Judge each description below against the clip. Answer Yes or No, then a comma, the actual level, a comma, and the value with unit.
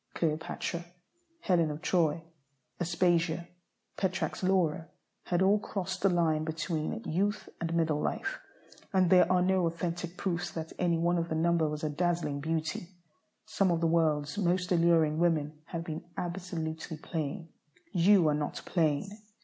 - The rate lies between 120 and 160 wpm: Yes, average, 150 wpm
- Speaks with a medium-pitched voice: Yes, medium, 170 Hz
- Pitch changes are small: Yes, narrow, 2.1 semitones